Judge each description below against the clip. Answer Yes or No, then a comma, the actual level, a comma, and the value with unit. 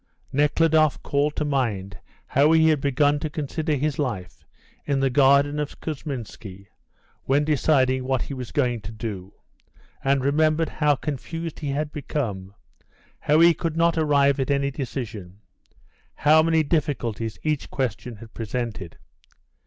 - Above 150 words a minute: No, average, 145 wpm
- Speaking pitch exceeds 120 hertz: Yes, medium, 140 Hz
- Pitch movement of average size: Yes, average, 3.8 semitones